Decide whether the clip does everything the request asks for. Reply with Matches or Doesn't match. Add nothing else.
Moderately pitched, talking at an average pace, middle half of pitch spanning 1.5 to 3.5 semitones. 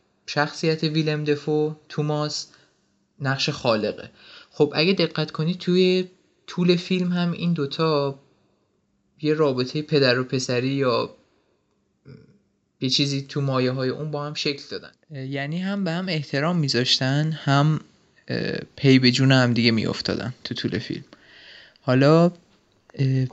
Matches